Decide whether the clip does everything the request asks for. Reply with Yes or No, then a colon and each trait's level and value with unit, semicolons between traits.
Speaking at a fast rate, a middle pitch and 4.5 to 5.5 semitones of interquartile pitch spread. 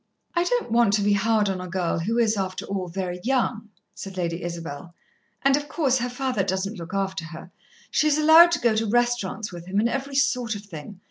No: fast, 220 wpm; high, 205 Hz; average, 5.0 semitones